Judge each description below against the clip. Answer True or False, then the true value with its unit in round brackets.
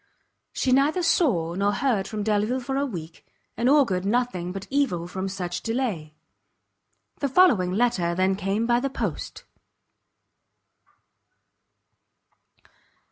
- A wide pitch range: True (6.0 semitones)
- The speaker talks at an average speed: False (120 wpm)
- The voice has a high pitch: True (210 Hz)